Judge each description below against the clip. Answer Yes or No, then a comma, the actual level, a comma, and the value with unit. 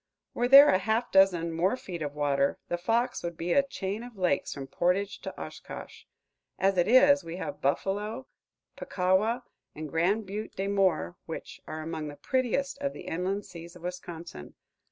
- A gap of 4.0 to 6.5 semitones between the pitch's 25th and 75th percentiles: Yes, average, 4.9 semitones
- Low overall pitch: No, high, 190 Hz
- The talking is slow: No, average, 175 wpm